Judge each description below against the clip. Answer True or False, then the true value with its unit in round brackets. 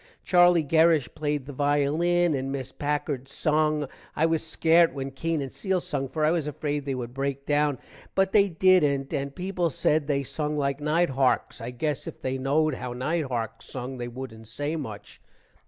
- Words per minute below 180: False (190 wpm)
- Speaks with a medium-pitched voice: True (145 Hz)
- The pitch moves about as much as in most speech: True (3.2 semitones)